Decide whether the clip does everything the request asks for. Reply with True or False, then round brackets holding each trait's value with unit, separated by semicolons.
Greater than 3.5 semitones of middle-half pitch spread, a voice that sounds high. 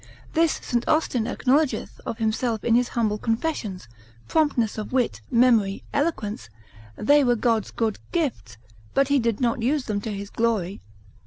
True (4.0 semitones; 235 Hz)